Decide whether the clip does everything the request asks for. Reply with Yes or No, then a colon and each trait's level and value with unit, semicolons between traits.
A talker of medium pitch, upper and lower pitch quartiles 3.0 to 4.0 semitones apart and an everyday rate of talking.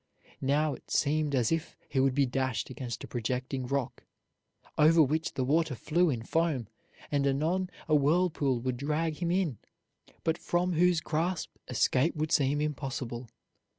Yes: medium, 145 Hz; average, 3.7 semitones; average, 150 wpm